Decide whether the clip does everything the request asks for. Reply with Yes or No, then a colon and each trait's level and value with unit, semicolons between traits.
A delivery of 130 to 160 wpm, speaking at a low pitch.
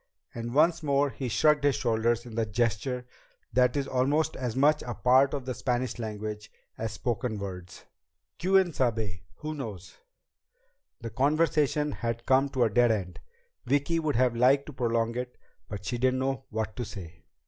No: average, 170 wpm; low, 125 Hz